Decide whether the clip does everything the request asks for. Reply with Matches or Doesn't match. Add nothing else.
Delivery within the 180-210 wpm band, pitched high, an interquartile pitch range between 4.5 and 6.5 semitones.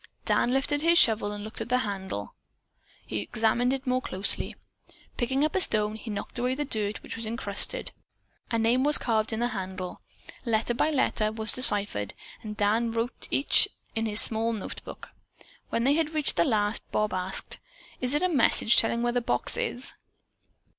Doesn't match